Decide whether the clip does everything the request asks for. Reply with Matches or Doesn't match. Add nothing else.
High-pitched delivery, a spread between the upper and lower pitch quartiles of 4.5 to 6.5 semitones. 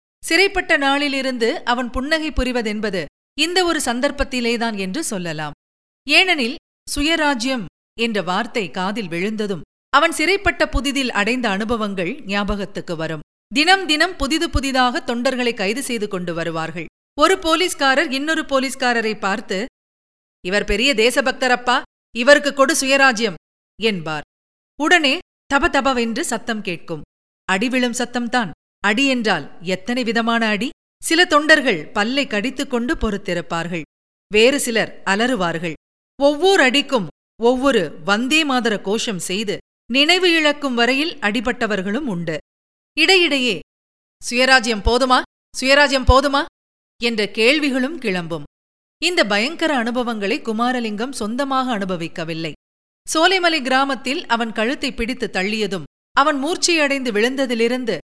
Matches